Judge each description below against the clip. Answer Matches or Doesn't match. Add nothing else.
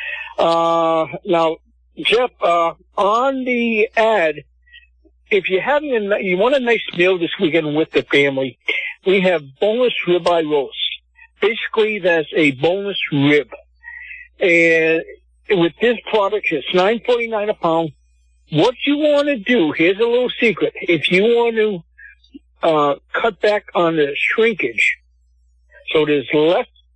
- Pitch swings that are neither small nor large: Doesn't match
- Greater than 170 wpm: Doesn't match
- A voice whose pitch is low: Doesn't match